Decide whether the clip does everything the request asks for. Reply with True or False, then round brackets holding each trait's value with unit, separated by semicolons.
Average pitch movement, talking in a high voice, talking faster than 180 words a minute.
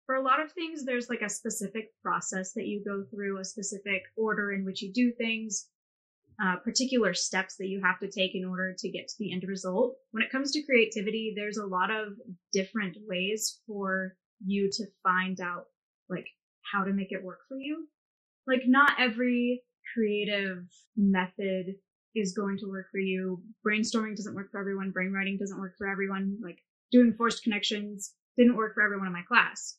True (3.1 semitones; 205 Hz; 190 wpm)